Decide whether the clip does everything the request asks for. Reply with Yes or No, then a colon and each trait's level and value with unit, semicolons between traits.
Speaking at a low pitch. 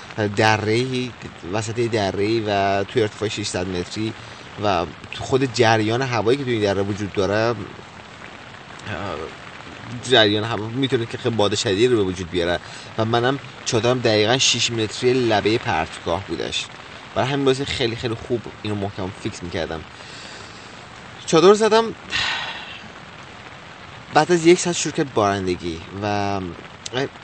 Yes: low, 110 Hz